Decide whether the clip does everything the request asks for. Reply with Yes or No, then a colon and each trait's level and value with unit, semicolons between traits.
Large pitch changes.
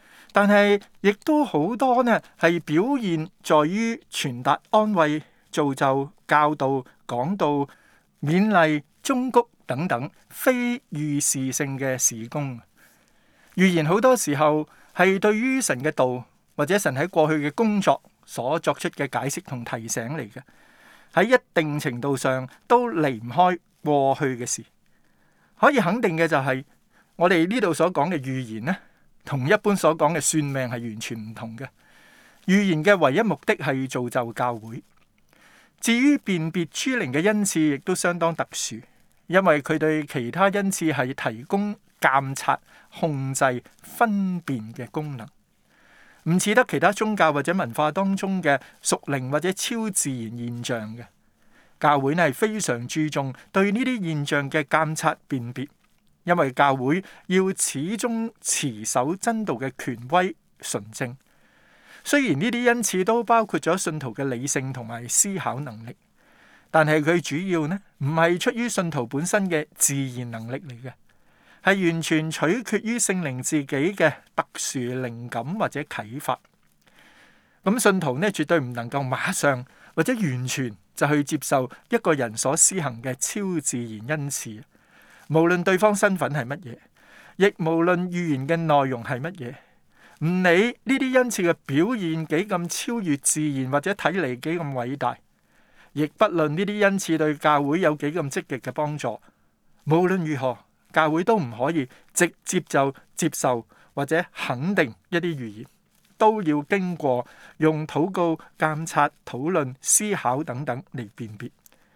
Yes: wide, 6.1 semitones